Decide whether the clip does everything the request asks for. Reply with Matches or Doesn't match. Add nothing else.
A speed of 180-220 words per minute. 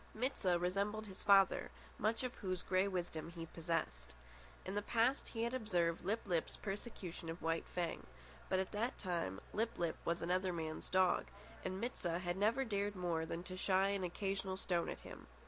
Matches